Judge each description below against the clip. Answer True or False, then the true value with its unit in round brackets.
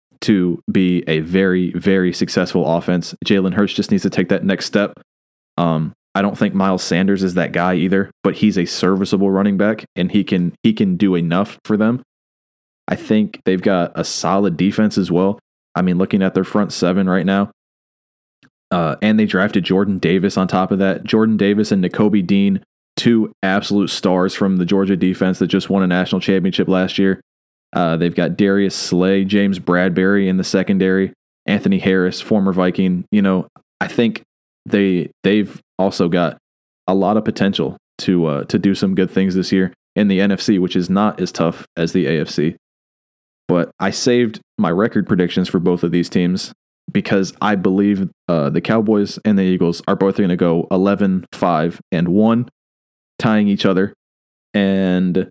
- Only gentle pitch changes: True (1.9 semitones)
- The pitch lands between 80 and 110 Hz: True (95 Hz)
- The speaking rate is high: False (185 wpm)